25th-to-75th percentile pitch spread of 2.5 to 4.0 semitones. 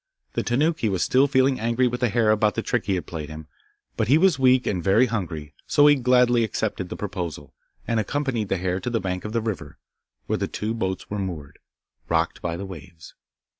No: average, 5.2 semitones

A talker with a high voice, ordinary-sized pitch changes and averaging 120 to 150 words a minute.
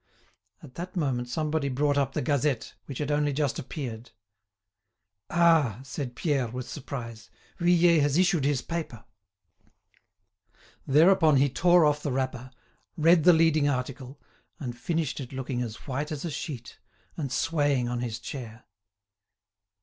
No: medium, 140 Hz; average, 3.9 semitones; average, 140 wpm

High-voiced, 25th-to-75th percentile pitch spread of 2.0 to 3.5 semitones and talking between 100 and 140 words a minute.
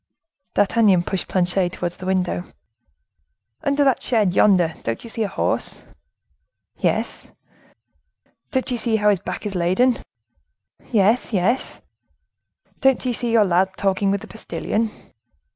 No: high, 200 Hz; average, 4.0 semitones; slow, 135 wpm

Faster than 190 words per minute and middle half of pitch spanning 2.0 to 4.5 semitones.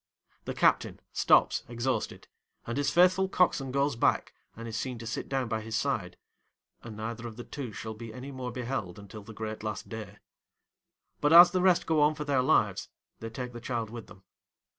Yes: average, 200 wpm; average, 4.0 semitones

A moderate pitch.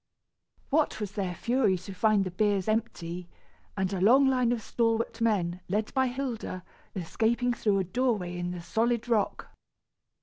No: high, 215 Hz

